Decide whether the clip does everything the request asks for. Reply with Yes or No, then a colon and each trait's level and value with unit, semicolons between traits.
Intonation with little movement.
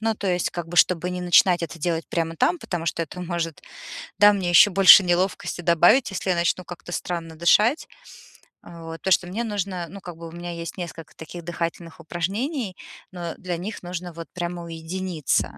Yes: narrow, 1.8 semitones